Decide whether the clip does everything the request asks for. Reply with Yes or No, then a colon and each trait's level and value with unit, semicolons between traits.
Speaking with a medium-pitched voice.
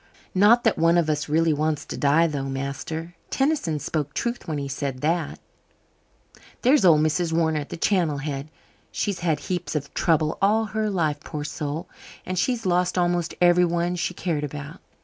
Yes: medium, 165 Hz